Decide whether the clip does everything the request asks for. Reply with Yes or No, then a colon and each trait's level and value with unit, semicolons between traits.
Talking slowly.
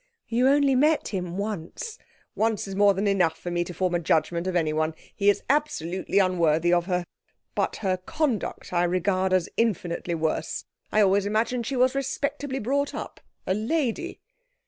No: average, 170 wpm